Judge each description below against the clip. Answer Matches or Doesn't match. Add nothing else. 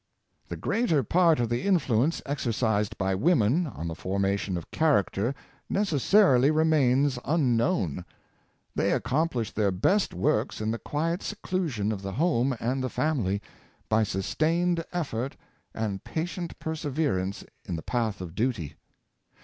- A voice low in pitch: Matches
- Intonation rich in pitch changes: Matches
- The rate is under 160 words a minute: Matches